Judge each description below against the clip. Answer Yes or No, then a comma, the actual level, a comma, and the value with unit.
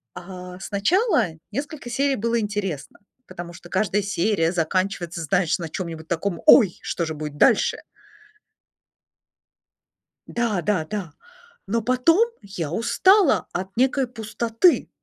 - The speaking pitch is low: No, high, 200 Hz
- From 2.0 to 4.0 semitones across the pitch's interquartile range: No, wide, 5.4 semitones